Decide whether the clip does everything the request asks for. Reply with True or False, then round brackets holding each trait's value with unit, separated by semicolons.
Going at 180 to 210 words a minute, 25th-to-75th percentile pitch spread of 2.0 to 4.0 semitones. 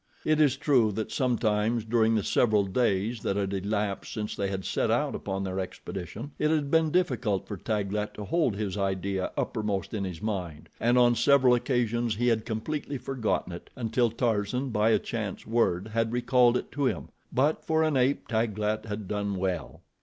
True (185 wpm; 3.6 semitones)